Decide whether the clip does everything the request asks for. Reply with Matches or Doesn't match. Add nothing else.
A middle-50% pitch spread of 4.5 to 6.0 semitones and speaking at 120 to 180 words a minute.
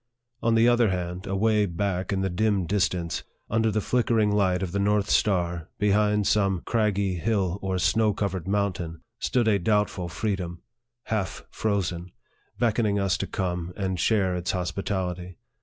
Doesn't match